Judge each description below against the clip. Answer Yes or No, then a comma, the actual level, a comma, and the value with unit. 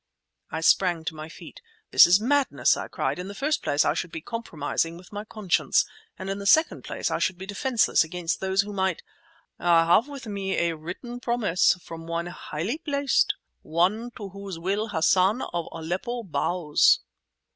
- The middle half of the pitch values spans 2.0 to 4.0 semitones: No, average, 4.6 semitones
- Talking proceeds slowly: No, average, 180 wpm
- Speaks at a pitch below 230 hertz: Yes, high, 190 Hz